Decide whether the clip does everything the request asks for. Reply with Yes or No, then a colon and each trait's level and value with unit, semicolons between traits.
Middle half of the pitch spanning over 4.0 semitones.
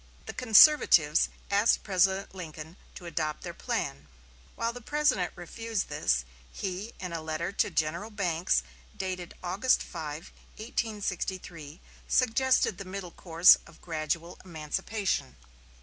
Yes: average, 4.4 semitones